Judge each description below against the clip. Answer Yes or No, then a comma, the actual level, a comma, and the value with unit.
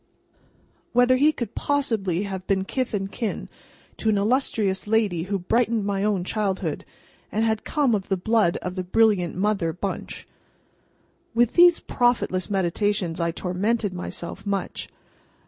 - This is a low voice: No, high, 205 Hz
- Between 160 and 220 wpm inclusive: No, average, 145 wpm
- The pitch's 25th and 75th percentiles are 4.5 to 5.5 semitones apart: No, average, 3.5 semitones